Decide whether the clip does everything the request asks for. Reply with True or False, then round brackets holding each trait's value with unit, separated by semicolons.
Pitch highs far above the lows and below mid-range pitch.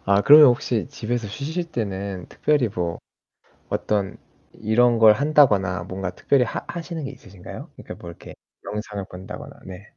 True (6.1 semitones; 110 Hz)